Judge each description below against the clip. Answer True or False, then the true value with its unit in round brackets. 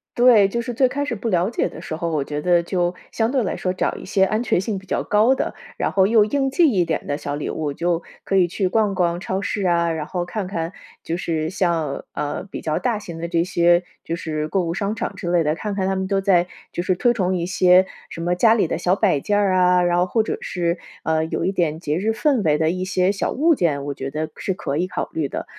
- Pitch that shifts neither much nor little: True (3.5 semitones)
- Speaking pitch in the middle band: True (180 Hz)